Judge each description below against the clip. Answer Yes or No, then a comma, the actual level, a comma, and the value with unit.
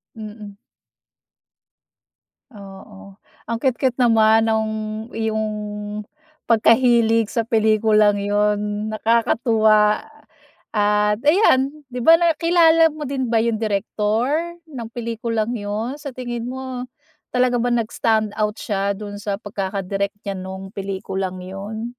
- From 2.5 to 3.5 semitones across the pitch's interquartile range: Yes, average, 2.9 semitones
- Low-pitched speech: No, high, 220 Hz